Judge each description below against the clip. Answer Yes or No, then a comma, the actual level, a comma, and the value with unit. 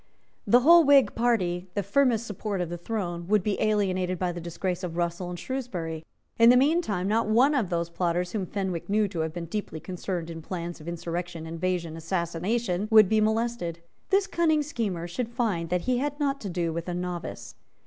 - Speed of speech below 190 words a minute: No, average, 200 wpm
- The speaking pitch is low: No, medium, 185 Hz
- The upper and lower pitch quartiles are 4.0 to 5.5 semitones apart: Yes, average, 5.0 semitones